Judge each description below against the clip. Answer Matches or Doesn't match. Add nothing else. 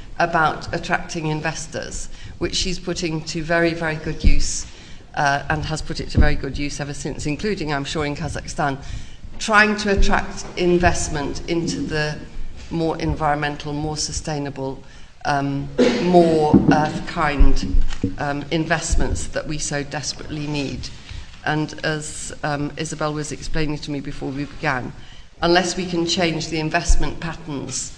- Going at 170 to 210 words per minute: Doesn't match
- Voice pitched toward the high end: Doesn't match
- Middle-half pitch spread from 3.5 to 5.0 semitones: Doesn't match